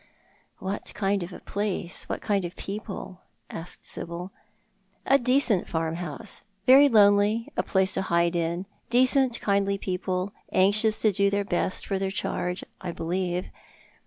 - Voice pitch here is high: Yes, high, 195 Hz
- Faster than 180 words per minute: No, average, 155 wpm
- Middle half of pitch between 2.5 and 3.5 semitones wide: Yes, average, 2.8 semitones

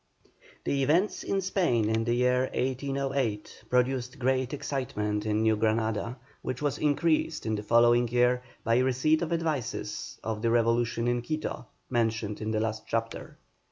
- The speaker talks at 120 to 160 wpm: Yes, average, 155 wpm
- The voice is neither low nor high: No, low, 120 Hz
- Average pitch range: Yes, average, 3.4 semitones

